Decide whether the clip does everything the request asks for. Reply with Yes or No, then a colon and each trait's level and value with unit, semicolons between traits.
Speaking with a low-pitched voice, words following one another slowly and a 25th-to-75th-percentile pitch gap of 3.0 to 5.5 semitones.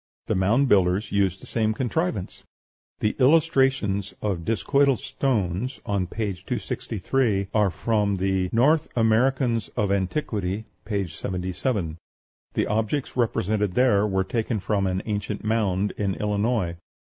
Yes: low, 105 Hz; slow, 125 wpm; average, 3.8 semitones